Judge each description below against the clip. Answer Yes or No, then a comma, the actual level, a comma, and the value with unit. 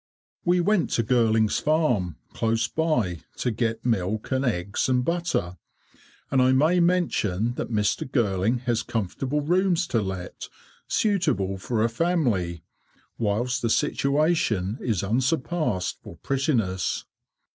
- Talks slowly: Yes, slow, 125 wpm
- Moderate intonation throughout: No, wide, 6.8 semitones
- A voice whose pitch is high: No, low, 120 Hz